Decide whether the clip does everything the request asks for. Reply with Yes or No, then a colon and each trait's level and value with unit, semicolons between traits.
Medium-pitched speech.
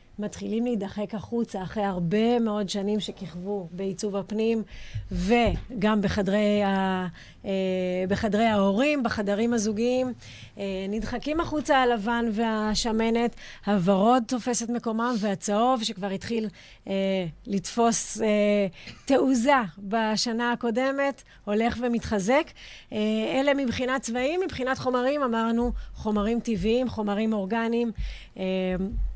No: high, 220 Hz